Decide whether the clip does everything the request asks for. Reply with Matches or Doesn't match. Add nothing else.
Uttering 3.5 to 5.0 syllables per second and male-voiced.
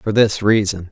Matches